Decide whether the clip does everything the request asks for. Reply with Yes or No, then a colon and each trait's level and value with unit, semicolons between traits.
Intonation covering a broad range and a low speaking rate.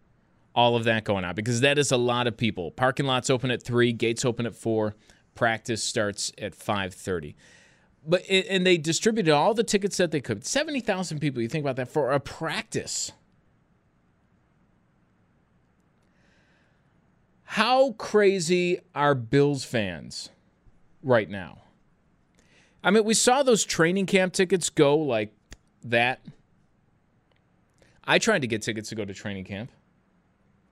No: wide, 8.2 semitones; average, 145 wpm